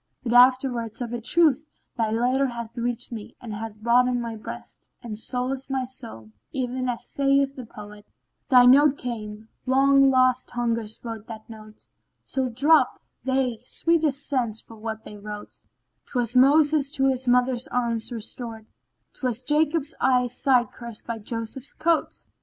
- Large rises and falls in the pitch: No, average, 2.8 semitones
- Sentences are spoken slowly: No, average, 160 wpm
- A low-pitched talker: No, high, 245 Hz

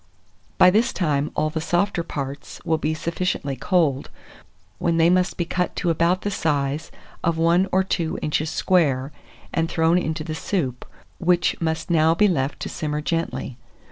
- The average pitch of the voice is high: No, medium, 165 Hz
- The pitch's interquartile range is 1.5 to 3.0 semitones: Yes, average, 2.7 semitones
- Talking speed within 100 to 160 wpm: No, average, 170 wpm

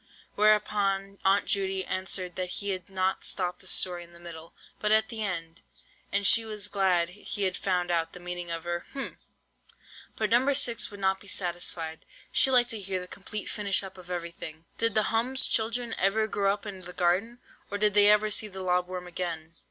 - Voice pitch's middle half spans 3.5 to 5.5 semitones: No, average, 2.9 semitones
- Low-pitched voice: No, high, 195 Hz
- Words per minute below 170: No, average, 200 wpm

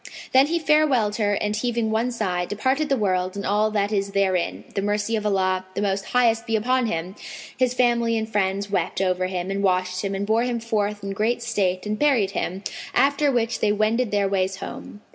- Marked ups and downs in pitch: No, average, 3.3 semitones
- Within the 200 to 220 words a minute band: Yes, fast, 205 wpm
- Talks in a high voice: Yes, high, 210 Hz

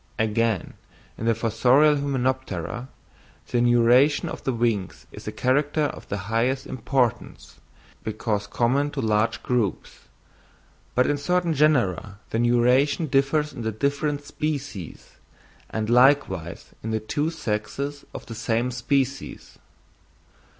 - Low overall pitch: Yes, low, 125 Hz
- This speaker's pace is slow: Yes, slow, 125 wpm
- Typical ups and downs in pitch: Yes, average, 4.2 semitones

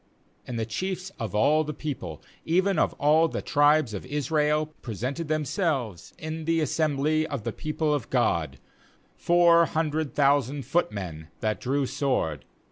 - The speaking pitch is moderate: Yes, medium, 145 Hz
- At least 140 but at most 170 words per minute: Yes, average, 150 wpm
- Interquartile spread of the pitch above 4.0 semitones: Yes, average, 4.4 semitones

